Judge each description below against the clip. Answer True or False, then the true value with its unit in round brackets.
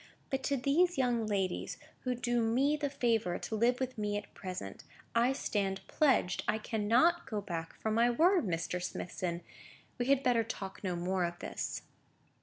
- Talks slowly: False (175 wpm)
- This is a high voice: True (225 Hz)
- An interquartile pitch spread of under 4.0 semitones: False (5.1 semitones)